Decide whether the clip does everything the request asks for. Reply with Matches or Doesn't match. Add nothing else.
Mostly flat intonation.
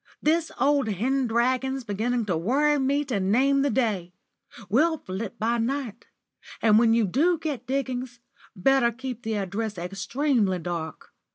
Doesn't match